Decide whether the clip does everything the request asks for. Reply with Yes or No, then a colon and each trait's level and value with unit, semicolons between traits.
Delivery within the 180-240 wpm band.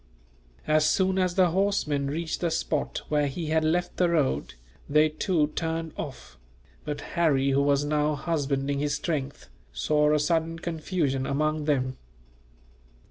No: average, 145 wpm